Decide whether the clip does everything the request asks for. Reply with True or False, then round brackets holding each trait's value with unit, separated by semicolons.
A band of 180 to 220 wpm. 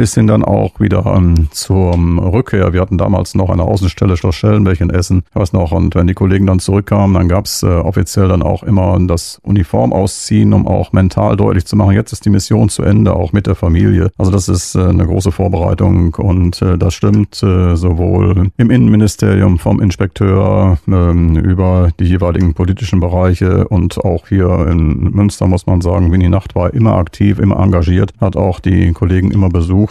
True (190 wpm)